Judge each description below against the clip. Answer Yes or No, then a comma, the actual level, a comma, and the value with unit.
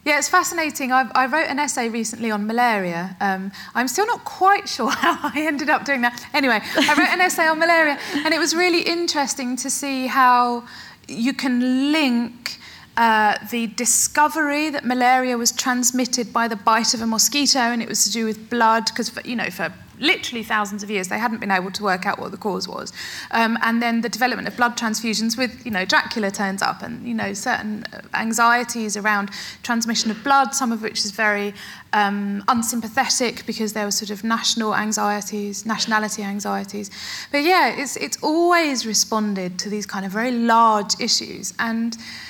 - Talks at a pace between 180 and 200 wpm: Yes, average, 190 wpm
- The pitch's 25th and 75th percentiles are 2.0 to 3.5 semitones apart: No, average, 4.1 semitones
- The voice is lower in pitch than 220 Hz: No, high, 235 Hz